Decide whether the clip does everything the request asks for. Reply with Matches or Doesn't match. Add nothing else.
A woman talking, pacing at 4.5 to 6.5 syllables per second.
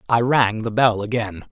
Doesn't match